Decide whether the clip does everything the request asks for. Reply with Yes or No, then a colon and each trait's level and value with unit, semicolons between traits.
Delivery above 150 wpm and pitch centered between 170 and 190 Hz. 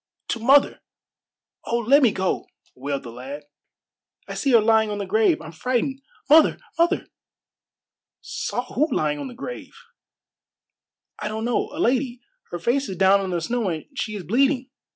No: average, 170 wpm; high, 225 Hz